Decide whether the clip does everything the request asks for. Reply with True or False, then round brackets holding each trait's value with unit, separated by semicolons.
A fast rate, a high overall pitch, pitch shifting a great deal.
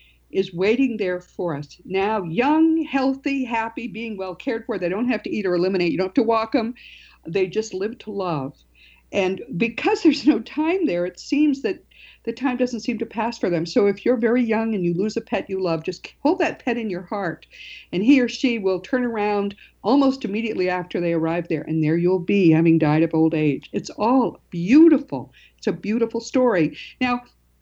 True (210 wpm; 215 Hz; 5.9 semitones)